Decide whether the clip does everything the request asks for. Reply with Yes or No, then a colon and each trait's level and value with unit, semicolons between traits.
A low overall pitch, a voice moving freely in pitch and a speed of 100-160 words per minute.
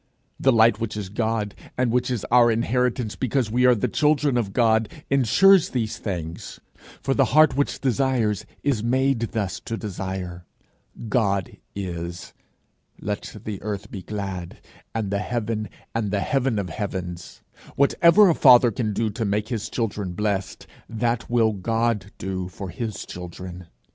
No: low, 110 Hz; average, 3.8 semitones; average, 155 wpm